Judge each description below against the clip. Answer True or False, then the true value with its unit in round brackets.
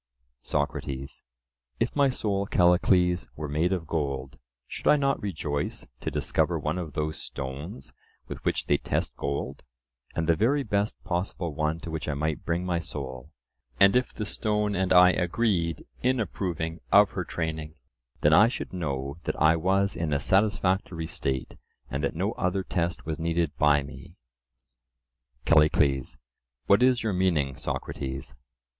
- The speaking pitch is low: True (85 Hz)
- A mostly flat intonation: False (4.5 semitones)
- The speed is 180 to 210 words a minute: False (155 wpm)